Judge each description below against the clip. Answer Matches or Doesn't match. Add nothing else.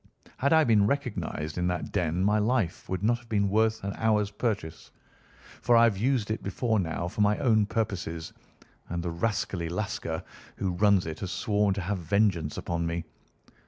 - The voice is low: Matches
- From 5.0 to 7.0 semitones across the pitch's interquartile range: Doesn't match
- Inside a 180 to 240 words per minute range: Matches